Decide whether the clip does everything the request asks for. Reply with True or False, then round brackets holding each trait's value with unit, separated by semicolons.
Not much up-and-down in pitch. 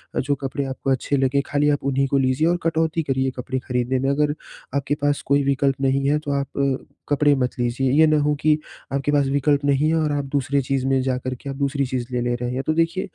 True (1.7 semitones)